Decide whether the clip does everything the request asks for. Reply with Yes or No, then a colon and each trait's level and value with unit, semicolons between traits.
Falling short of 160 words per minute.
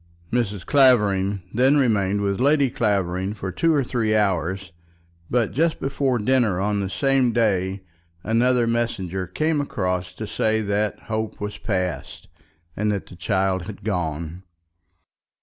Yes: average, 140 wpm